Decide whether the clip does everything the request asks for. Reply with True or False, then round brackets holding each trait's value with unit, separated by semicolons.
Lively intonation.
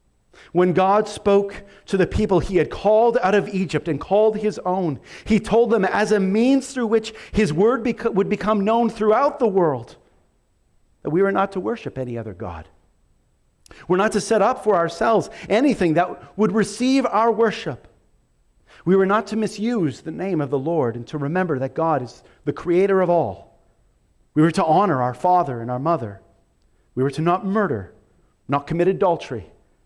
True (6.6 semitones)